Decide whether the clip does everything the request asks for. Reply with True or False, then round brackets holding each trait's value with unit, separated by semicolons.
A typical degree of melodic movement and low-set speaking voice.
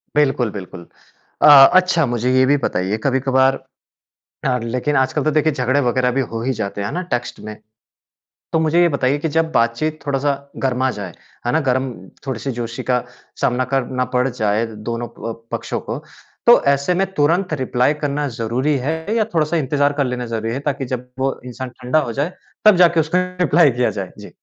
True (3.5 semitones; 130 Hz)